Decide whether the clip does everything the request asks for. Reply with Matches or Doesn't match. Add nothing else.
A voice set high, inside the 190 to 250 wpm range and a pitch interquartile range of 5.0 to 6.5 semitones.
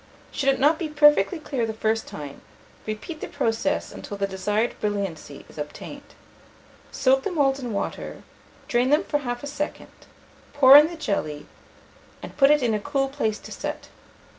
Doesn't match